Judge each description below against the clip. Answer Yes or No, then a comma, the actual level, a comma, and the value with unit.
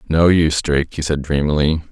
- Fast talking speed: No, average, 190 wpm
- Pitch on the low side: Yes, very low, 75 Hz